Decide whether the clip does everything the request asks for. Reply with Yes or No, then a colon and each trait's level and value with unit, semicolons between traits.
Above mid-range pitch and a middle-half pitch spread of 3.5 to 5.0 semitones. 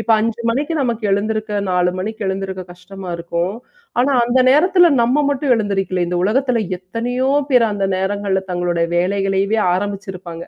Yes: high, 205 Hz; average, 4.1 semitones